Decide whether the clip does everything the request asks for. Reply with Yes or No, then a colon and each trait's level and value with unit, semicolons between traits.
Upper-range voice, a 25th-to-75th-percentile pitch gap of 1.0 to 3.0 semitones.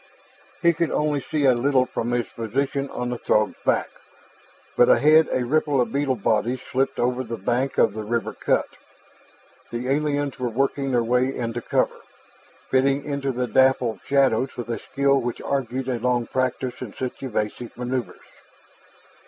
No: low, 130 Hz; narrow, 2.4 semitones